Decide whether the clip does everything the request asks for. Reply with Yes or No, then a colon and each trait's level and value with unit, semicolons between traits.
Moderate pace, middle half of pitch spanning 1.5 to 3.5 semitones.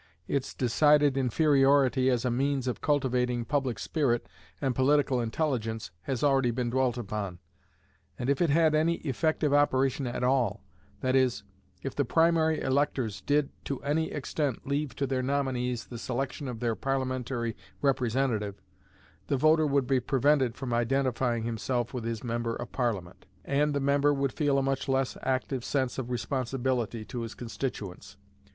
Yes: average, 160 wpm; average, 2.7 semitones